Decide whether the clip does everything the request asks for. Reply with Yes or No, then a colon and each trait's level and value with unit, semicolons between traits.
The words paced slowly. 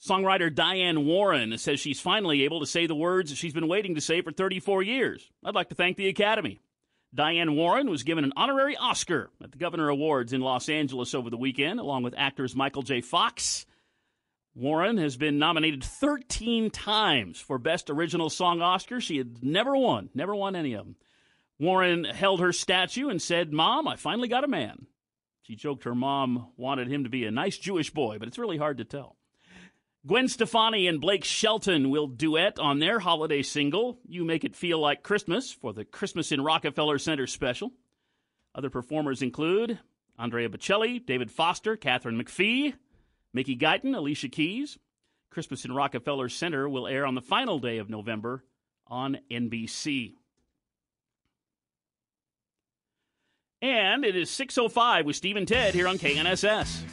No: average, 170 wpm